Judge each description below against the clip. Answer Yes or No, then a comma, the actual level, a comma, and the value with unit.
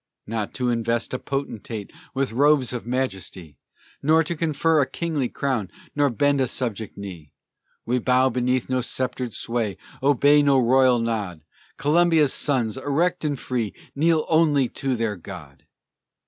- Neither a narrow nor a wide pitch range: Yes, average, 4.0 semitones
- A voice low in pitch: Yes, low, 130 Hz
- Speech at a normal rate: Yes, average, 145 wpm